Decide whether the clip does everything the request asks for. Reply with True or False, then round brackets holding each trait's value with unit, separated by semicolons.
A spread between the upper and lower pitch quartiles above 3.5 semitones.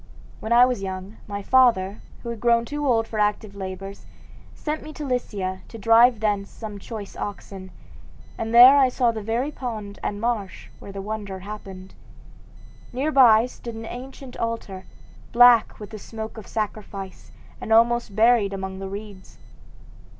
False (3.2 semitones)